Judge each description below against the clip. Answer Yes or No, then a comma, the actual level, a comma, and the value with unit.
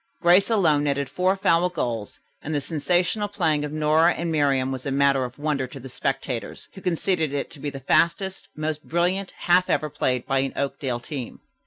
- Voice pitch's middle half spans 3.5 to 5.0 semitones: Yes, average, 4.2 semitones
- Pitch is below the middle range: No, medium, 150 Hz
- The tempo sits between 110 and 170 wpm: No, average, 195 wpm